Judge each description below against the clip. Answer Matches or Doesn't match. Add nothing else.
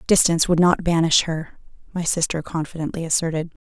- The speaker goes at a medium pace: Matches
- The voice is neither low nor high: Matches